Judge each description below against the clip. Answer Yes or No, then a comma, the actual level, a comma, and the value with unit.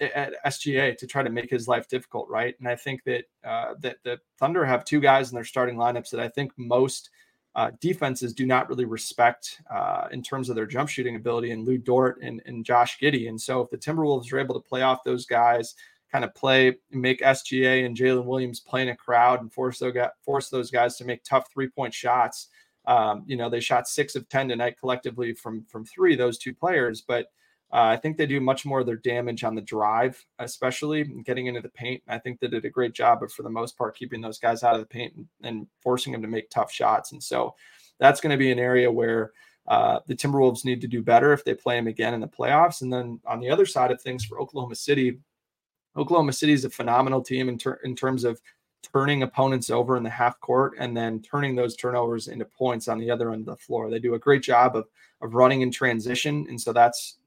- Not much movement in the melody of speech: Yes, narrow, 1.9 semitones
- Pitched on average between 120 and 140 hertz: Yes, low, 125 Hz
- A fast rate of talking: Yes, fast, 240 wpm